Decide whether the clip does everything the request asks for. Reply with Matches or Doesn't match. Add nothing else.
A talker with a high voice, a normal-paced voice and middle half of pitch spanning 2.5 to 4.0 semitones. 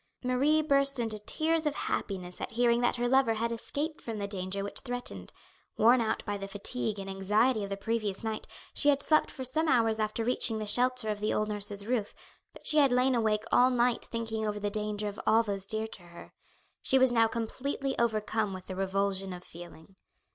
Doesn't match